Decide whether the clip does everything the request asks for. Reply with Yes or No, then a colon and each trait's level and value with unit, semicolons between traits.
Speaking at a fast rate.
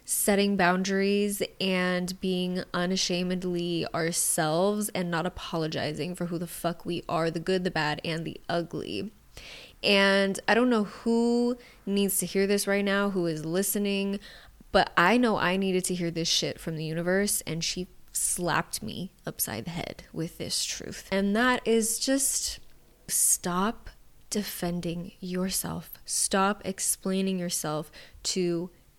No: average, 145 wpm